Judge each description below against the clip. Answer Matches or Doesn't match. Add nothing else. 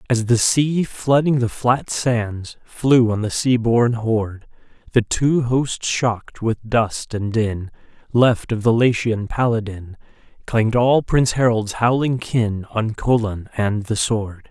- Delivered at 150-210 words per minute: Matches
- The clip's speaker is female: Doesn't match